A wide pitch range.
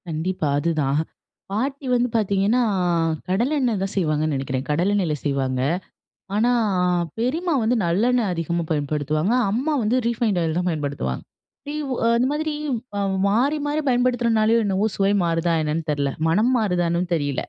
Yes: wide, 7.2 semitones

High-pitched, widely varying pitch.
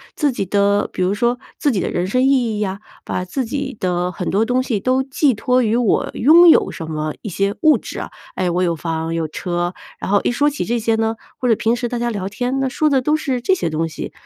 Yes: high, 225 Hz; wide, 5.8 semitones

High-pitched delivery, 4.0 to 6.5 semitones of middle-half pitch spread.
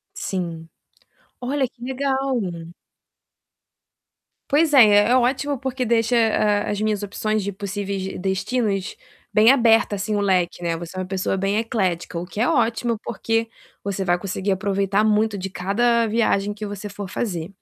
No: high, 205 Hz; average, 3.4 semitones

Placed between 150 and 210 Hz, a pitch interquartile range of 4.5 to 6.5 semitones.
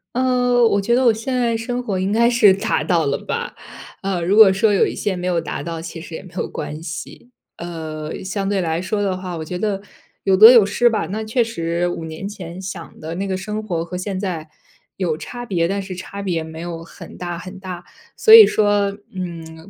No: high, 190 Hz; average, 4.0 semitones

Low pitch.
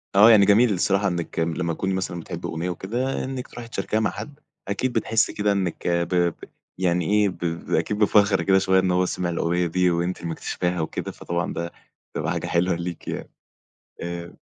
Yes: very low, 90 Hz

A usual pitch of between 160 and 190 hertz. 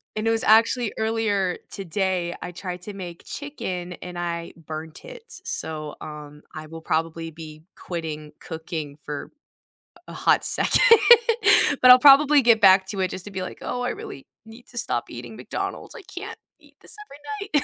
Yes: medium, 185 Hz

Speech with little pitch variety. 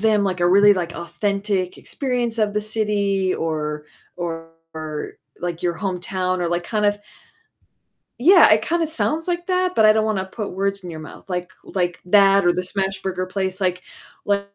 No: average, 3.0 semitones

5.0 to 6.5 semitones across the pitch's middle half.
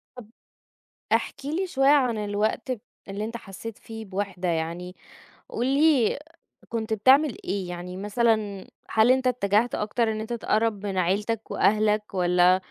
No: average, 3.4 semitones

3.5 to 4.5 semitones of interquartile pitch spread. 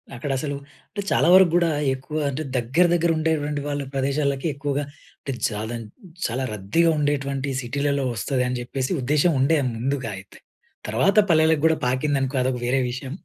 No: average, 2.9 semitones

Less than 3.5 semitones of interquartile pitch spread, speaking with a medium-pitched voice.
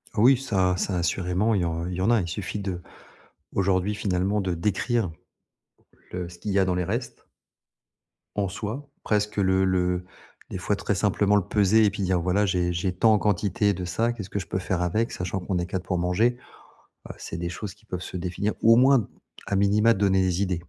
No: narrow, 2.5 semitones; very low, 95 Hz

